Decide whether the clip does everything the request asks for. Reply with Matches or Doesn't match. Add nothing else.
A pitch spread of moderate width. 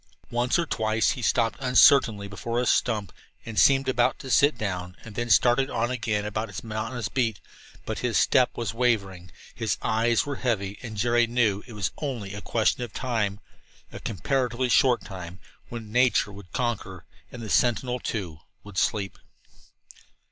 Matches